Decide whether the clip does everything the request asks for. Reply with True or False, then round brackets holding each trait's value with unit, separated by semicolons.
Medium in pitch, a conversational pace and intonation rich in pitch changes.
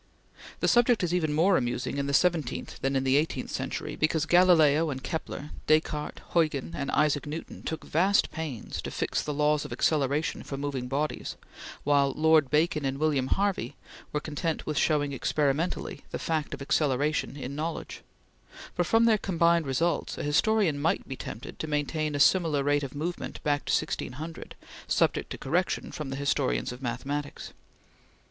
False (150 Hz; 170 wpm; 2.7 semitones)